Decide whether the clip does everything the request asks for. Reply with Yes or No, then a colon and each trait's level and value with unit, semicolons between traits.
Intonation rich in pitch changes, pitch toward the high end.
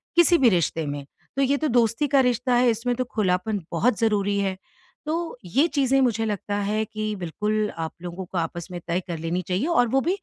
Yes: wide, 5.7 semitones; high, 215 Hz